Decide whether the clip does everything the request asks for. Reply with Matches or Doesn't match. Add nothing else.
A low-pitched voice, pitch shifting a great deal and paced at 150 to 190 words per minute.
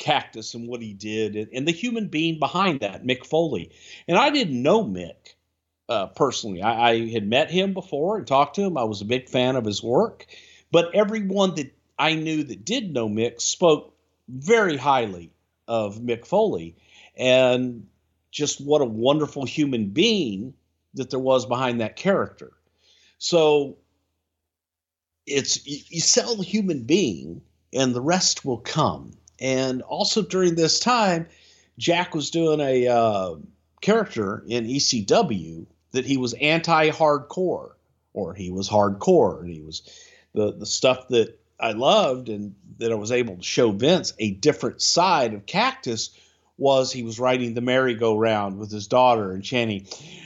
Matches